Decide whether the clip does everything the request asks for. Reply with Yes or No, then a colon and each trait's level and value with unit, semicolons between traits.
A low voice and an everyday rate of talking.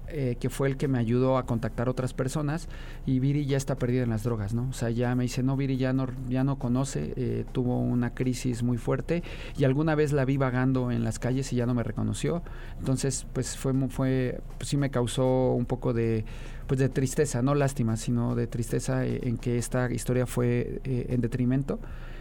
No: low, 130 Hz; fast, 215 wpm